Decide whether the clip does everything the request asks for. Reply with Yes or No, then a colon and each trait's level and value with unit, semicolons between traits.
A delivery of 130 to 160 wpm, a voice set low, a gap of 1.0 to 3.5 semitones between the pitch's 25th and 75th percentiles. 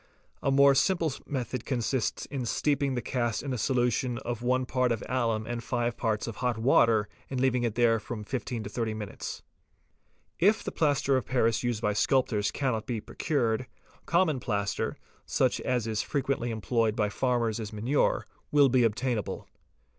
No: average, 175 wpm; low, 120 Hz; average, 2.9 semitones